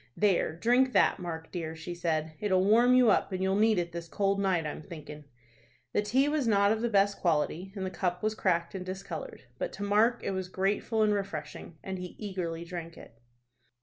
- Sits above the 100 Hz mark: Yes, high, 190 Hz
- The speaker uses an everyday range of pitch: Yes, average, 3.5 semitones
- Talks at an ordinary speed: No, fast, 210 wpm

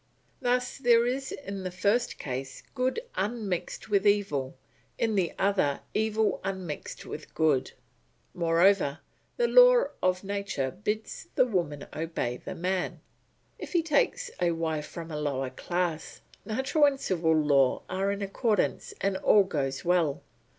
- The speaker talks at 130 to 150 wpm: Yes, average, 145 wpm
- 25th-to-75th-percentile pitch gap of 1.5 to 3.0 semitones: No, wide, 5.6 semitones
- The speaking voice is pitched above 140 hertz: Yes, high, 190 Hz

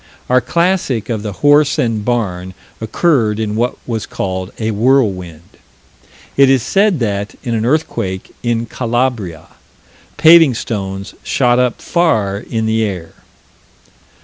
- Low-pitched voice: Yes, low, 115 Hz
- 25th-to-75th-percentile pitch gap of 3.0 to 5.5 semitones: Yes, average, 4.6 semitones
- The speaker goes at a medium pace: No, slow, 130 wpm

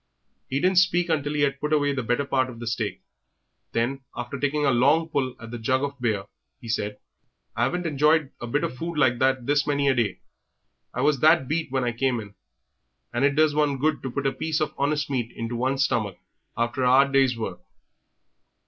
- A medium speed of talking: No, fast, 220 wpm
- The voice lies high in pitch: No, low, 135 Hz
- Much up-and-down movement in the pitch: No, average, 3.4 semitones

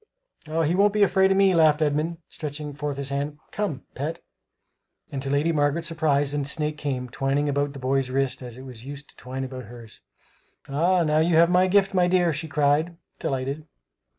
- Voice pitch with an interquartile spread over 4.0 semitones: No, average, 3.4 semitones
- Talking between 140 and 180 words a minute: No, average, 190 wpm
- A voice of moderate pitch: Yes, medium, 145 Hz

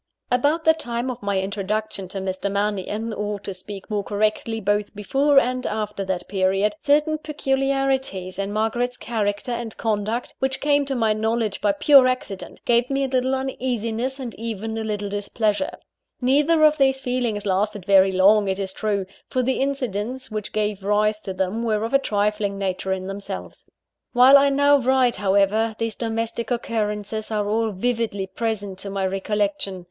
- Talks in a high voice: Yes, high, 215 Hz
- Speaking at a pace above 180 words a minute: No, average, 170 wpm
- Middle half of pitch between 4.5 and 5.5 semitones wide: No, average, 3.9 semitones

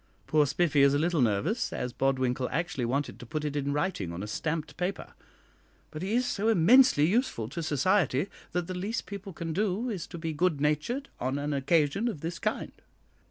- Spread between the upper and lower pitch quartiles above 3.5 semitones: Yes, average, 5.2 semitones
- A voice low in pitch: No, medium, 160 Hz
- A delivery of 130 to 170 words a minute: No, average, 200 wpm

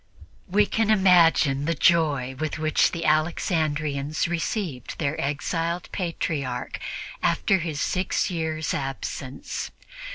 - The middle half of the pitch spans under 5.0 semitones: Yes, average, 3.2 semitones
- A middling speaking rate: No, slow, 105 wpm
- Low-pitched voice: No, medium, 160 Hz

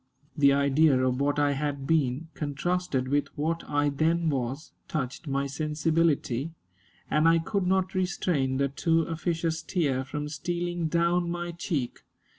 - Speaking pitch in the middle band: Yes, medium, 155 Hz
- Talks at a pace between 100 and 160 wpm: Yes, average, 145 wpm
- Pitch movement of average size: Yes, average, 3.3 semitones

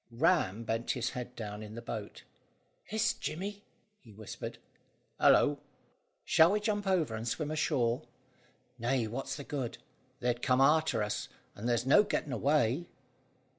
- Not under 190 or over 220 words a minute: No, average, 145 wpm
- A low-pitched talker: Yes, low, 125 Hz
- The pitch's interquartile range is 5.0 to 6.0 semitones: Yes, average, 5.3 semitones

